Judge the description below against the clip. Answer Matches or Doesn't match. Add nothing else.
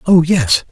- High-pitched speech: Doesn't match